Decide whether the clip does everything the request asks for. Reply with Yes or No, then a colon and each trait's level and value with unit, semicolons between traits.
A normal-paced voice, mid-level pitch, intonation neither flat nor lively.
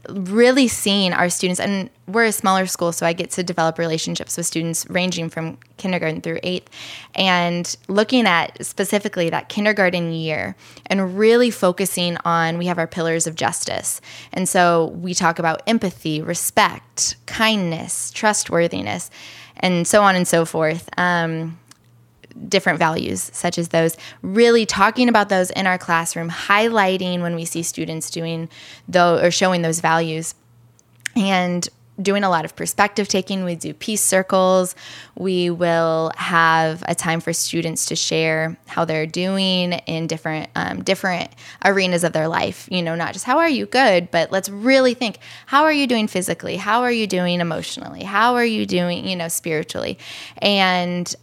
Yes: average, 165 wpm; medium, 175 Hz; average, 3.0 semitones